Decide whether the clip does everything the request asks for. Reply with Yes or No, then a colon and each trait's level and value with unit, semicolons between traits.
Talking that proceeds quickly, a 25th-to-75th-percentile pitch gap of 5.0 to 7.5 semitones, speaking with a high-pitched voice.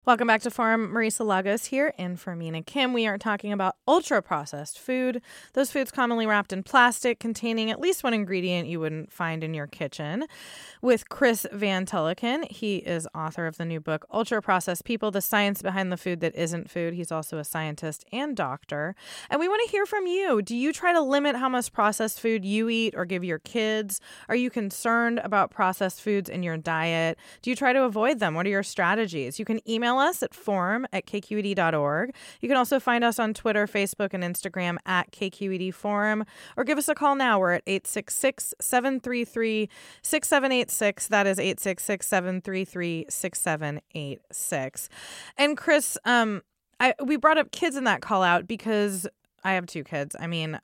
No: average, 185 wpm; wide, 5.4 semitones; high, 210 Hz